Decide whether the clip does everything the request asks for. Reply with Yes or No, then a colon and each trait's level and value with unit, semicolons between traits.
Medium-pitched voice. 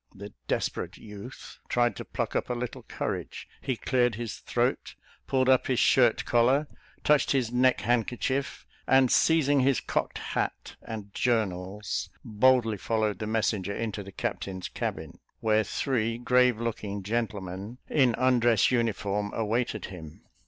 No: low, 115 Hz